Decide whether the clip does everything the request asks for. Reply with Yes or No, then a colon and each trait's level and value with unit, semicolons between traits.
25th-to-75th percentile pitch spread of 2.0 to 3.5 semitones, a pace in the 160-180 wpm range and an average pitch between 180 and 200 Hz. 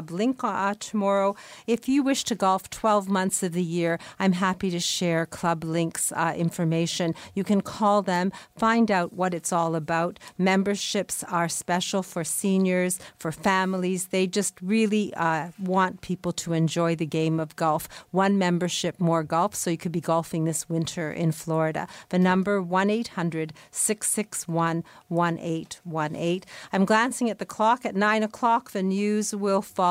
Yes: average, 3.1 semitones; average, 165 wpm; medium, 185 Hz